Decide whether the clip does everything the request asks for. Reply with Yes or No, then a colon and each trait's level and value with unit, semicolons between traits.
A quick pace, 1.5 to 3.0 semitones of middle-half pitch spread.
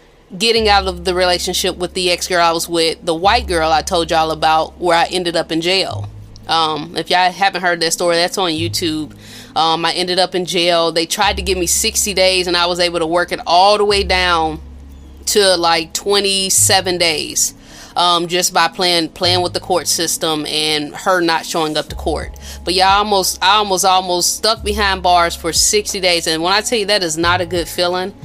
Yes: fast, 215 wpm; narrow, 2.4 semitones